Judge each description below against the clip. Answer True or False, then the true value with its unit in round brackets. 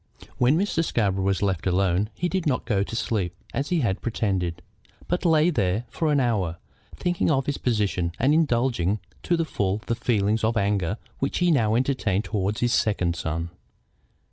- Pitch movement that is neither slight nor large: False (6.3 semitones)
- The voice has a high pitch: False (110 Hz)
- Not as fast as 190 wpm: True (180 wpm)